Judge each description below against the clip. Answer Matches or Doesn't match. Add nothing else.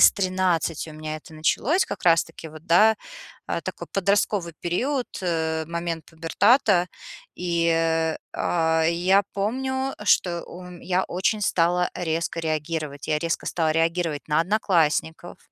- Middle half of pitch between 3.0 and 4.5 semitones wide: Doesn't match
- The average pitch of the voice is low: Doesn't match